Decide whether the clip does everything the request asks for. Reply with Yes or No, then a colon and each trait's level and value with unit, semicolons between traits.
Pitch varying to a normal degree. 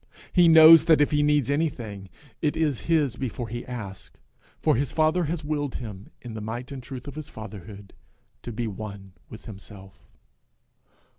No: wide, 5.7 semitones